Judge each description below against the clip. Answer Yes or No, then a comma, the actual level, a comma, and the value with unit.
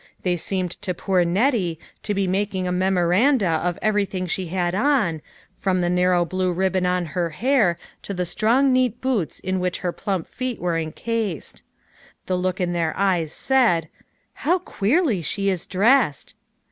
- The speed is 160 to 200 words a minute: Yes, average, 170 wpm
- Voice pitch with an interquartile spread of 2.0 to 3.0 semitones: No, average, 3.4 semitones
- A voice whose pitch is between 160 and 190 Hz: Yes, medium, 185 Hz